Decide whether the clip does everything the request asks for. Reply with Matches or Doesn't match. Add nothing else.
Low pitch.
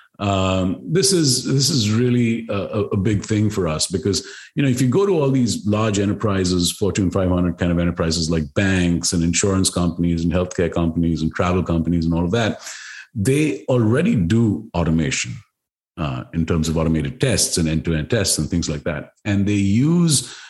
Matches